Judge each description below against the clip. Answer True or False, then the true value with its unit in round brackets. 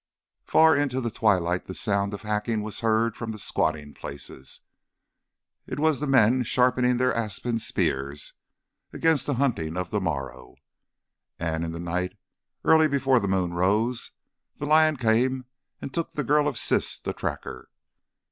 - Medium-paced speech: True (155 wpm)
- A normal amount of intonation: False (6.6 semitones)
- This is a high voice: False (110 Hz)